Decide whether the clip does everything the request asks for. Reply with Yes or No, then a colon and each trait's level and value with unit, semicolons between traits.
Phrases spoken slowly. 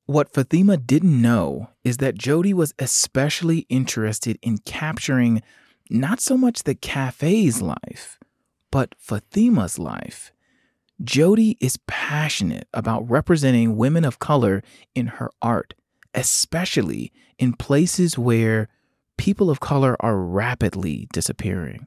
Yes: slow, 115 wpm